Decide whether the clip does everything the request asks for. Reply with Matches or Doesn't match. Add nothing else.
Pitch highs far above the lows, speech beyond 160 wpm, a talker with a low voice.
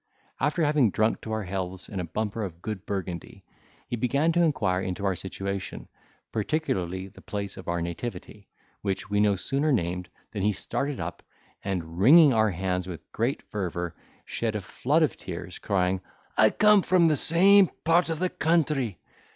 Matches